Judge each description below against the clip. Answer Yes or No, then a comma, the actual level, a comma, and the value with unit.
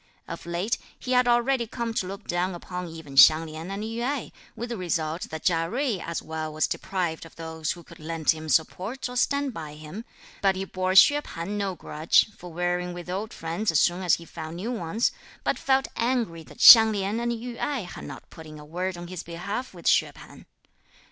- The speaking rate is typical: No, fast, 220 wpm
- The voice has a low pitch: No, medium, 180 Hz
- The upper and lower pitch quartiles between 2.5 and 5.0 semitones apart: No, wide, 5.5 semitones